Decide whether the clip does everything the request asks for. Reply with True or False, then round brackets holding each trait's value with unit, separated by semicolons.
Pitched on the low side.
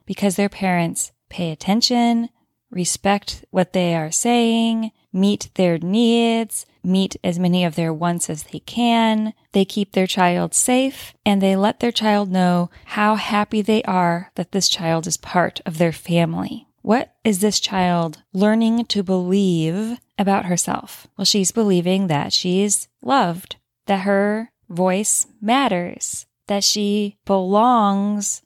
False (200 Hz)